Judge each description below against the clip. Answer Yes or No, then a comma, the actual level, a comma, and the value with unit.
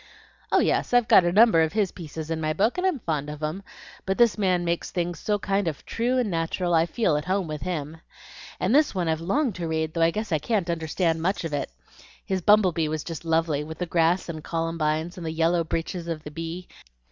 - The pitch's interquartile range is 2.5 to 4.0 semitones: Yes, average, 3.1 semitones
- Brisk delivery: Yes, fast, 240 wpm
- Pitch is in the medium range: Yes, medium, 170 Hz